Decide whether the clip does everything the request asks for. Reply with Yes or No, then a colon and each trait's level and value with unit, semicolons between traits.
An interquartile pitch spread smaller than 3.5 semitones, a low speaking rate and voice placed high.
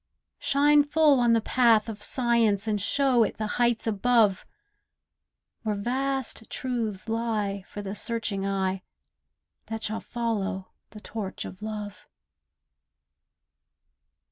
Yes: average, 2.8 semitones; slow, 115 wpm; high, 220 Hz